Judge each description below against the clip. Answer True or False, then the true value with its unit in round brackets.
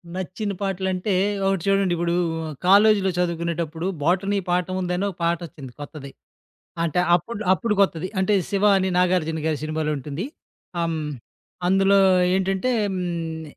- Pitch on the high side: False (180 Hz)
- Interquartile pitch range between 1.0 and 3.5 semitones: True (2.8 semitones)